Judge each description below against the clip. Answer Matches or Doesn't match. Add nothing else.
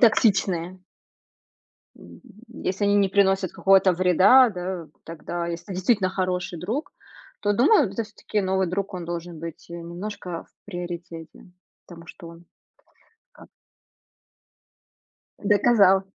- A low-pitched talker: Doesn't match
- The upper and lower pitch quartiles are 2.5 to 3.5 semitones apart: Matches